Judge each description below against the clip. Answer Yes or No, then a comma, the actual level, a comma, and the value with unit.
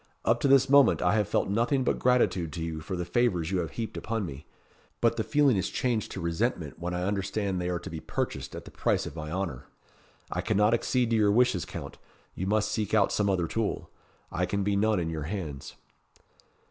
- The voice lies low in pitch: Yes, low, 100 Hz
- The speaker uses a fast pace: Yes, fast, 225 wpm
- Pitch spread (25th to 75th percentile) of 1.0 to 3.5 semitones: No, average, 4.4 semitones